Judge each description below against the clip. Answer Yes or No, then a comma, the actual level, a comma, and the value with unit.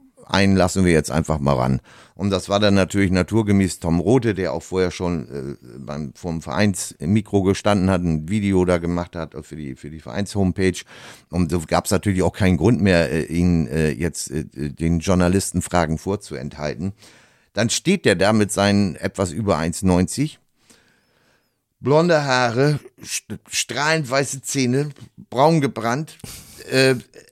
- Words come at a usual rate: Yes, average, 160 wpm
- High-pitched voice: No, very low, 95 Hz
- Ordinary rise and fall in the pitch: Yes, average, 4.1 semitones